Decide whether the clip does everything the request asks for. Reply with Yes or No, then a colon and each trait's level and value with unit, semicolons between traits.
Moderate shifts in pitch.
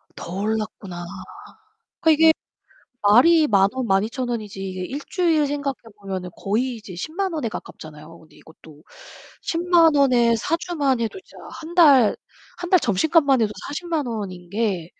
No: wide, 8.2 semitones